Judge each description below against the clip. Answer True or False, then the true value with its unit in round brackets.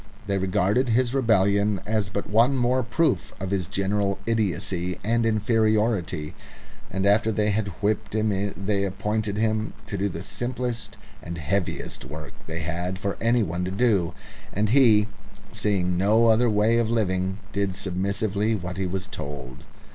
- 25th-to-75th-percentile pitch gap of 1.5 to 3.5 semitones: True (2.9 semitones)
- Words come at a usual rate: True (155 wpm)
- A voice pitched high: False (100 Hz)